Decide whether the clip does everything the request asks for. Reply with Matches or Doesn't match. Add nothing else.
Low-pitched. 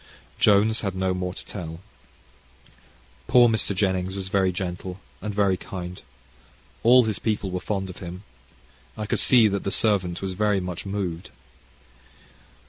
Matches